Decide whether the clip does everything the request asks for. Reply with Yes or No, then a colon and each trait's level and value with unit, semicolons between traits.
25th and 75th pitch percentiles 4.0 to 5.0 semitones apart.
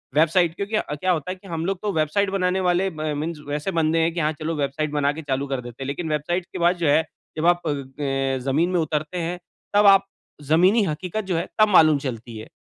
No: average, 3.4 semitones